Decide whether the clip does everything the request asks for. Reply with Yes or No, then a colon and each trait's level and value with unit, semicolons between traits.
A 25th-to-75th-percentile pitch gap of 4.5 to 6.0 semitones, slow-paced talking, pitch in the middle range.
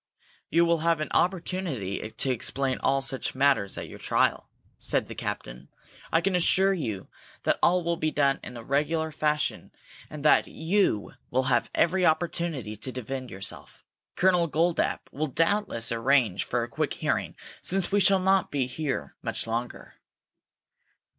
No: average, 5.2 semitones; average, 160 wpm; medium, 150 Hz